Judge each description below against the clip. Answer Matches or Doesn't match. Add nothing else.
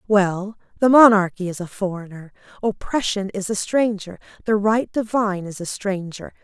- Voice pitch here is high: Matches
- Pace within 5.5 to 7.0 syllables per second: Doesn't match